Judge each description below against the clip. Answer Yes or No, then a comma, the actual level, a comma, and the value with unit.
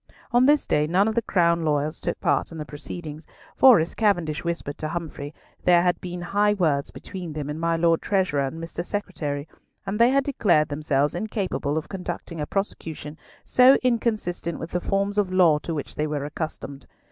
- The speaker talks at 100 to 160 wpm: No, average, 195 wpm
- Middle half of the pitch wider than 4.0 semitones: Yes, average, 4.5 semitones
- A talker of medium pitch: Yes, medium, 170 Hz